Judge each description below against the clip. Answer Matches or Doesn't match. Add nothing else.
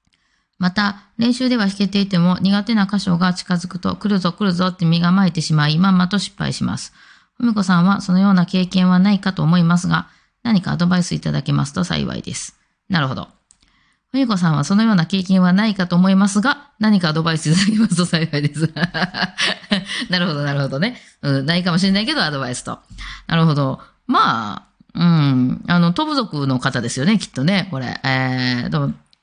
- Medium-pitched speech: Matches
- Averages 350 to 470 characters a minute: Matches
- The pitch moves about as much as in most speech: Matches